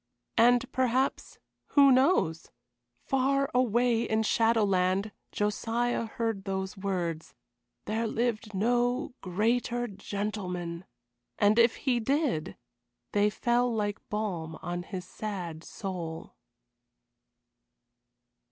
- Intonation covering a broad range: No, average, 4.2 semitones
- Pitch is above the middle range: Yes, high, 215 Hz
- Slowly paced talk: Yes, slow, 95 wpm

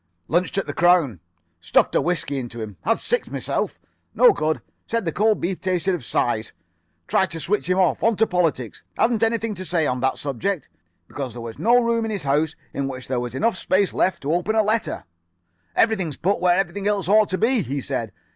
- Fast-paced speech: Yes, fast, 210 wpm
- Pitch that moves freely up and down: Yes, wide, 7.1 semitones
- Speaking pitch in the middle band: Yes, medium, 180 Hz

